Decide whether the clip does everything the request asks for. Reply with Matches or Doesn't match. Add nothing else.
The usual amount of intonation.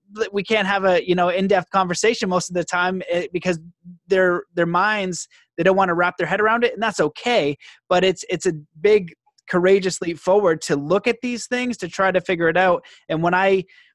Doesn't match